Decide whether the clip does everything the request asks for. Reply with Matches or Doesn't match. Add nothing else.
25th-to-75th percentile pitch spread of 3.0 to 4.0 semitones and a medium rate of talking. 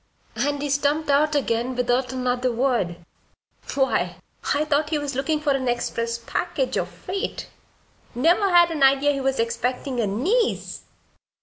Matches